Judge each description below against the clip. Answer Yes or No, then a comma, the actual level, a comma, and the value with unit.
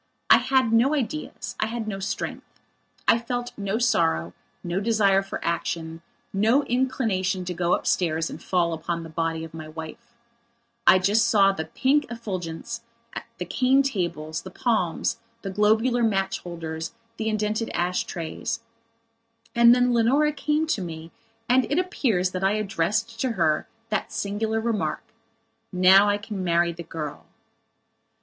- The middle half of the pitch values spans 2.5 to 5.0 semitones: No, wide, 5.4 semitones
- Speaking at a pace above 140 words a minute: Yes, average, 150 wpm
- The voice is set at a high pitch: Yes, high, 200 Hz